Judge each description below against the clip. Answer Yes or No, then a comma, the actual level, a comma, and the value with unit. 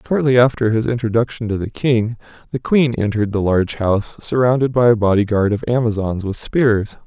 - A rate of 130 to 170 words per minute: No, average, 185 wpm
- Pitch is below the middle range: Yes, low, 115 Hz